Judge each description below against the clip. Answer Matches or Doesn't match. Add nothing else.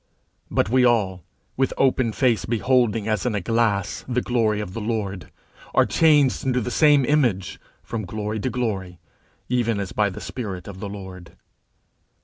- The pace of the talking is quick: Doesn't match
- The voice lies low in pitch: Matches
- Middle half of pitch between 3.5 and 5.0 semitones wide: Matches